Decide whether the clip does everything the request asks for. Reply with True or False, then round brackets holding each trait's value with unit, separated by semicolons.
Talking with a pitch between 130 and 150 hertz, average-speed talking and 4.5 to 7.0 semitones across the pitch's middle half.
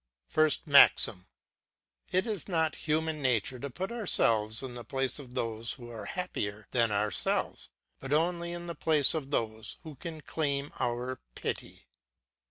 True (140 Hz; 160 wpm; 5.5 semitones)